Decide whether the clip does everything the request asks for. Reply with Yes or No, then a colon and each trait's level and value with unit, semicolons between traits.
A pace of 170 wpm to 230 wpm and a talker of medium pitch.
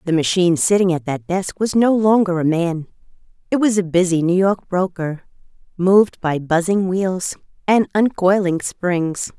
No: average, 160 wpm; medium, 180 Hz